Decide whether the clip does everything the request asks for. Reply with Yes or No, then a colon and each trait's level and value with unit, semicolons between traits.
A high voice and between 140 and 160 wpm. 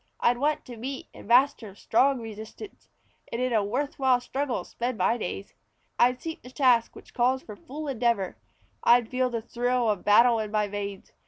No: high, 240 Hz; average, 185 wpm